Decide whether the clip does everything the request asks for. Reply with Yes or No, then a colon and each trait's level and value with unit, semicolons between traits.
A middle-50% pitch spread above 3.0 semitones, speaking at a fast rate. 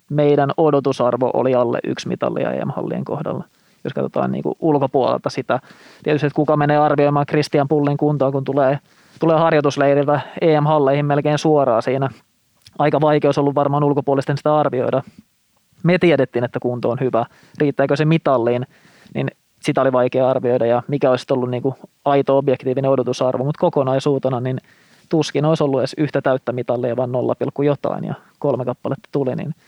No: narrow, 2.4 semitones; fast, 160 wpm